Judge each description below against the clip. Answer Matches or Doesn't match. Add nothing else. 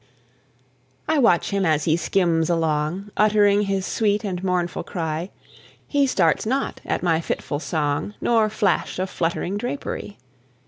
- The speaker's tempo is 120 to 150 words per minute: Matches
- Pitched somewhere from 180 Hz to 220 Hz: Matches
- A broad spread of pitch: Doesn't match